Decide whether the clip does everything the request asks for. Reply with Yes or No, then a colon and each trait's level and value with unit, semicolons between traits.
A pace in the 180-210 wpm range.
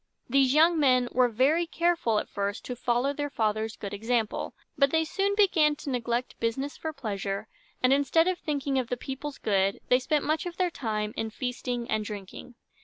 Yes: average, 190 wpm